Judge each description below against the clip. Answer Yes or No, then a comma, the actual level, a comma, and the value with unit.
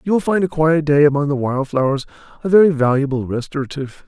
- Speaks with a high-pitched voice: No, medium, 145 Hz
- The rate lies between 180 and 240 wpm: Yes, fast, 205 wpm